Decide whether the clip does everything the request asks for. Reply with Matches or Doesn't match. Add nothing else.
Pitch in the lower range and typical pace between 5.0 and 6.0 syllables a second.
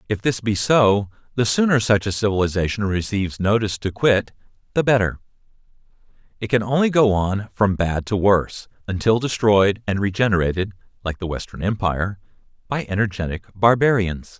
Matches